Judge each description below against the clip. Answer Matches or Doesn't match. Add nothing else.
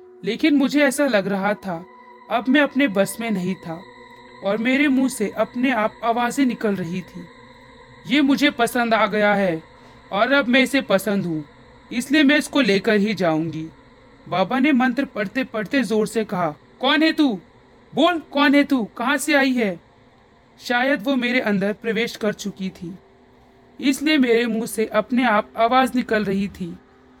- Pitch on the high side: Matches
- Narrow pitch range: Doesn't match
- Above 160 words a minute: Matches